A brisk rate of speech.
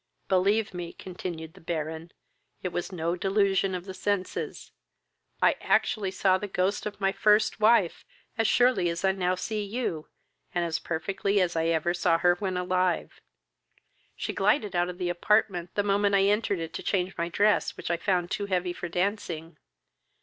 No: average, 180 wpm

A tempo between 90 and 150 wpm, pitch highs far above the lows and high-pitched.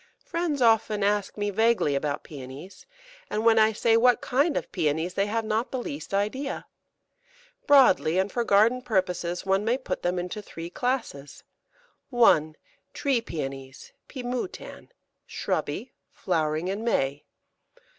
Yes: average, 140 wpm; wide, 5.9 semitones; high, 205 Hz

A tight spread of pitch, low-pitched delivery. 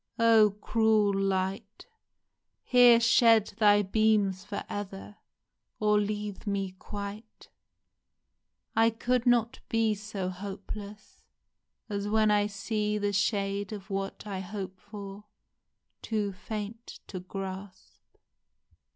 No: narrow, 1.8 semitones; high, 205 Hz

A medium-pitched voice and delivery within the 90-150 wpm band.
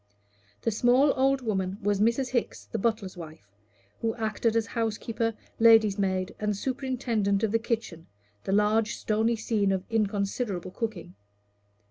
No: high, 215 Hz; average, 140 wpm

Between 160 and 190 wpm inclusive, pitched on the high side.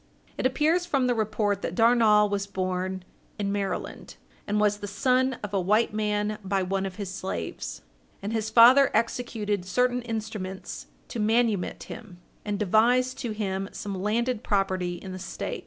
Yes: average, 165 wpm; high, 210 Hz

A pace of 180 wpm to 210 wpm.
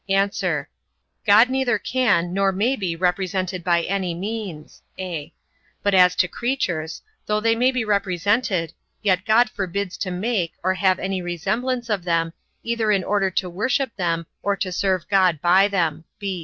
No: average, 160 wpm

